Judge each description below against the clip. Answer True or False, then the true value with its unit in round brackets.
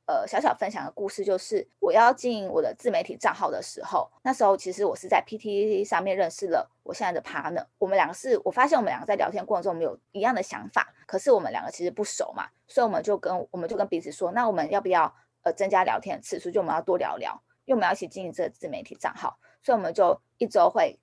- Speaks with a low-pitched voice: False (215 Hz)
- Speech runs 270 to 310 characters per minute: False (415 characters per minute)